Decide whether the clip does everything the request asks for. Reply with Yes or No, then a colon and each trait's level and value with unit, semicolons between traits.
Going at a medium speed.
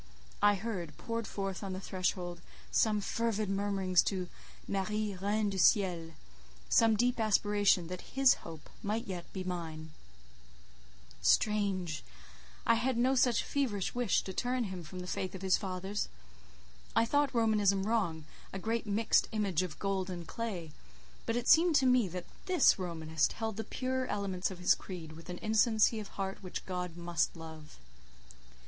Yes: average, 160 wpm